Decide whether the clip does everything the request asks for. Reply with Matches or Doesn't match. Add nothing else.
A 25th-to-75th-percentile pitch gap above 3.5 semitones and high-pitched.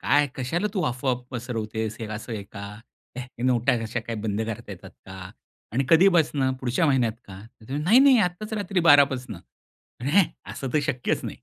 Doesn't match